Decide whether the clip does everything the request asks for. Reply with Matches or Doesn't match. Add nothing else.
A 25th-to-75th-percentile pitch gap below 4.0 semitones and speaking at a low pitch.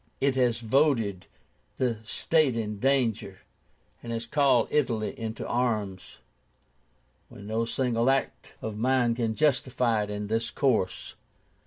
Matches